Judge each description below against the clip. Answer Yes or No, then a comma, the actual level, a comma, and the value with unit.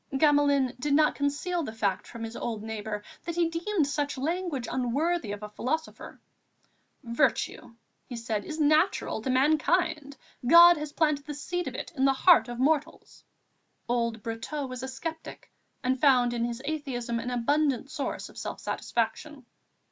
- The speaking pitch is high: Yes, very high, 275 Hz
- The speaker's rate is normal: Yes, average, 165 wpm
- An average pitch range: Yes, average, 4.6 semitones